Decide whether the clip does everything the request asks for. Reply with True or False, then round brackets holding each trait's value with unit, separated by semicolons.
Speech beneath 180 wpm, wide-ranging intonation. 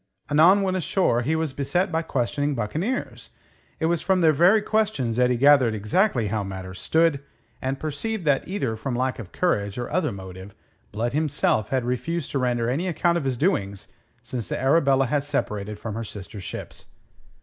False (185 wpm; 6.4 semitones)